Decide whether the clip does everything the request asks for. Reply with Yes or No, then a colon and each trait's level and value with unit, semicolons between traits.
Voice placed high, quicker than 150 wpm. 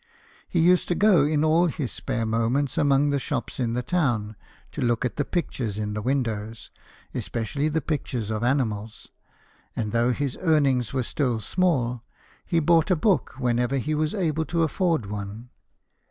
No: low, 135 Hz; average, 170 wpm